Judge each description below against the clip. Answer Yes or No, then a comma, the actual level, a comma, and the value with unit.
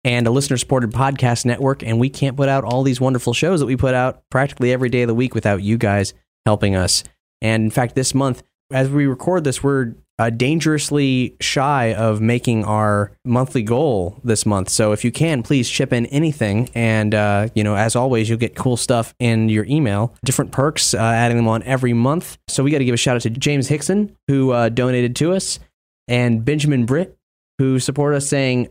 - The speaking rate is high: Yes, fast, 210 wpm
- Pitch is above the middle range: No, low, 125 Hz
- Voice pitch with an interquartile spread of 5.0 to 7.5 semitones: No, average, 3.2 semitones